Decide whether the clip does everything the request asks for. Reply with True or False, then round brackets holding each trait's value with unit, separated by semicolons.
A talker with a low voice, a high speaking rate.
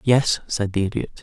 False (110 Hz; 195 wpm)